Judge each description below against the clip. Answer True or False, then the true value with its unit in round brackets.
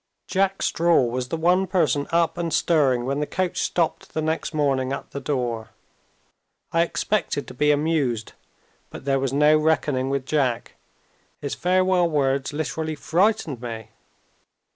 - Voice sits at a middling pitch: True (150 Hz)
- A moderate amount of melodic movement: True (3.9 semitones)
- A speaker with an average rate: True (150 wpm)